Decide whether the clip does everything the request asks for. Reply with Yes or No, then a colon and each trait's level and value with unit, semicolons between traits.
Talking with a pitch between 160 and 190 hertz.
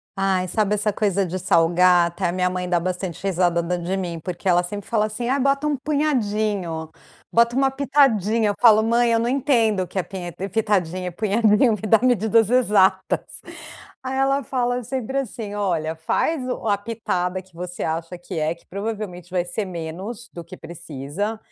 No: high, 200 Hz